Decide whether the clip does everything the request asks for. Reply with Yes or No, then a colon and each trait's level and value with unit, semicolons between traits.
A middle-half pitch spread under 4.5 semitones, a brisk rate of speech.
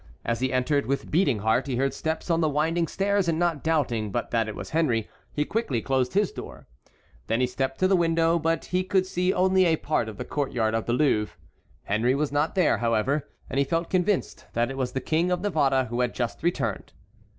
No: wide, 5.5 semitones; fast, 230 wpm